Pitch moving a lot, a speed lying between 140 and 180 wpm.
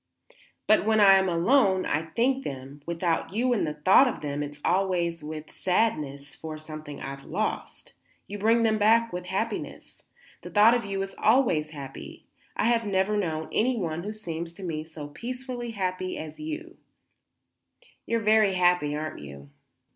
Yes: wide, 6.1 semitones; average, 170 wpm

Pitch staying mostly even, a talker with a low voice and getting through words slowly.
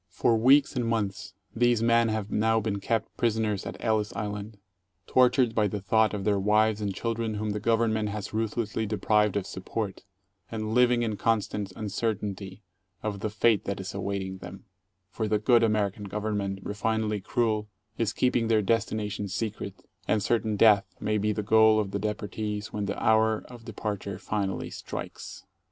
No: narrow, 1.6 semitones; low, 105 Hz; average, 175 wpm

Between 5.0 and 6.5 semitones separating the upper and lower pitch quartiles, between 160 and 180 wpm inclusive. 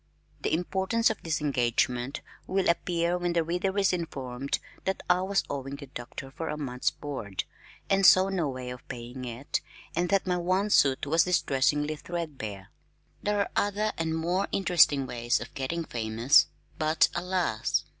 Yes: wide, 5.6 semitones; average, 165 wpm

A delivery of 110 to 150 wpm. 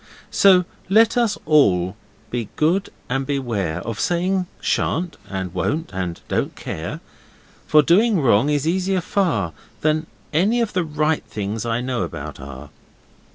Yes: average, 140 wpm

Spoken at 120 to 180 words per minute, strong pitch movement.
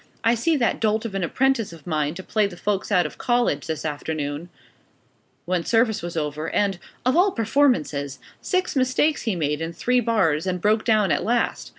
No: average, 195 wpm; wide, 6.7 semitones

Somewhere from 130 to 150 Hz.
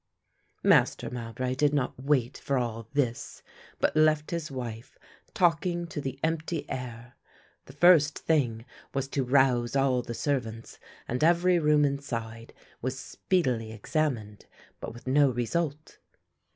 Yes: low, 135 Hz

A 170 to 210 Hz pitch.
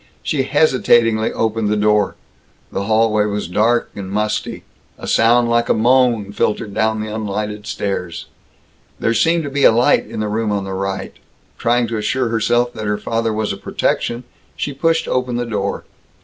No: low, 110 Hz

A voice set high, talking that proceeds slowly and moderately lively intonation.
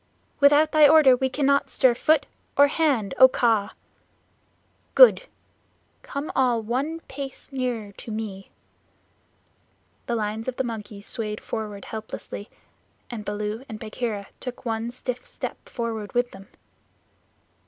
Yes: high, 240 Hz; slow, 130 wpm; average, 4.0 semitones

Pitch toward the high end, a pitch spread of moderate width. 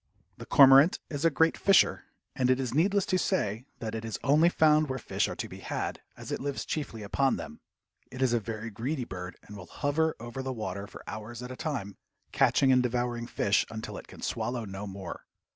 No: low, 125 Hz; average, 4.6 semitones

